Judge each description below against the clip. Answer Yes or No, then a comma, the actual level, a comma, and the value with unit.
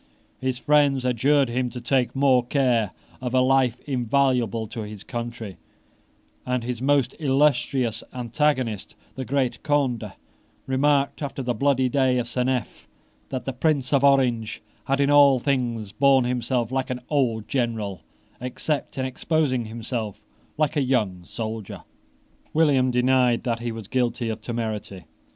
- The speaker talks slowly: No, average, 145 wpm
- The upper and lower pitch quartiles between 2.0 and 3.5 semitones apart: Yes, narrow, 2.6 semitones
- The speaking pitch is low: Yes, low, 125 Hz